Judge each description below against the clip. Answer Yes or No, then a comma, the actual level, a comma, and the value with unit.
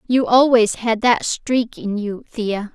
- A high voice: Yes, high, 225 Hz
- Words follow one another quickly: No, average, 175 wpm